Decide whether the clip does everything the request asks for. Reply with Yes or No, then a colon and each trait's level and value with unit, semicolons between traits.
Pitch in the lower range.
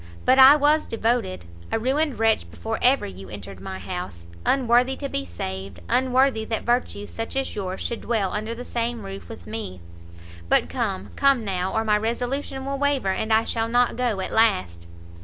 No: high, 225 Hz